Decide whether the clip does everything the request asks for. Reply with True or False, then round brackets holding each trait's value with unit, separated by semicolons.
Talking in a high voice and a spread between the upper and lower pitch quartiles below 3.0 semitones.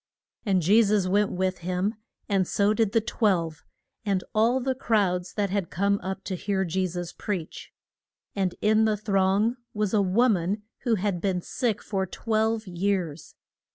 True (200 Hz; 2.6 semitones)